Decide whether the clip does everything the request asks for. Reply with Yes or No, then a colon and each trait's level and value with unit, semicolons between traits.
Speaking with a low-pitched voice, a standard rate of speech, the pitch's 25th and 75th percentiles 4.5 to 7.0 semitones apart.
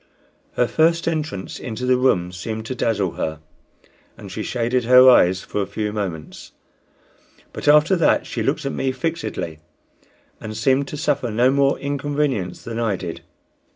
Yes: low, 125 Hz; average, 160 wpm; average, 5.3 semitones